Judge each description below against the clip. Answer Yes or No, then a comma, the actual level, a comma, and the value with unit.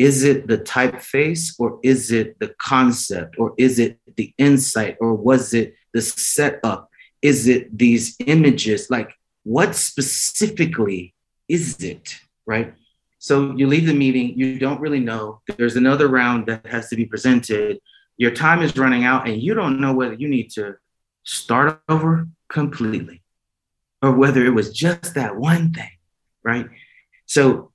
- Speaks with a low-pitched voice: Yes, low, 130 Hz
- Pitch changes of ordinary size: Yes, average, 3.9 semitones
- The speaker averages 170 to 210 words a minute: No, average, 155 wpm